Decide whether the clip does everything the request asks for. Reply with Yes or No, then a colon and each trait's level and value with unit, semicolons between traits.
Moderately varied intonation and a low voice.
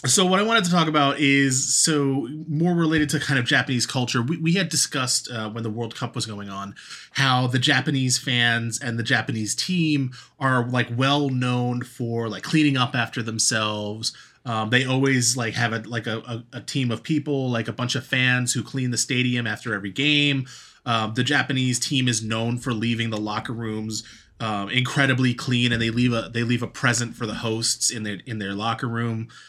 Yes: average, 3.0 semitones; low, 125 Hz